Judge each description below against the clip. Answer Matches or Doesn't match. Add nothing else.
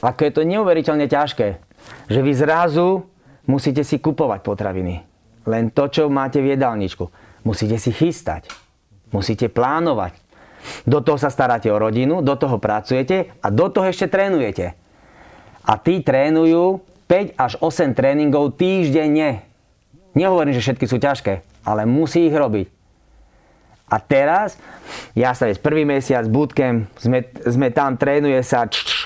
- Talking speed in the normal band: Matches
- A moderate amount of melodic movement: Doesn't match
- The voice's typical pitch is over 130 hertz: Matches